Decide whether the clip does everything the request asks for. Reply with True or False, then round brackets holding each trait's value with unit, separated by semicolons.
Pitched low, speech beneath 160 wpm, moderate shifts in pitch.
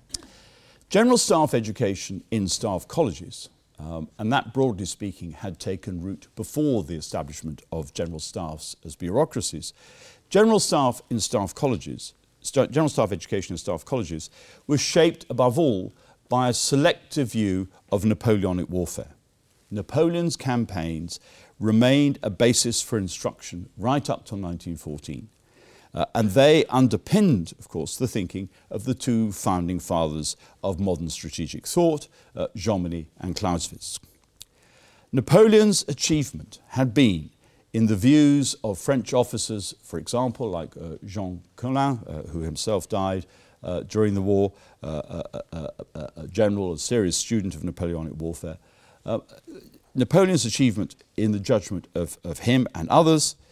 False (110 Hz; 140 wpm; 6.8 semitones)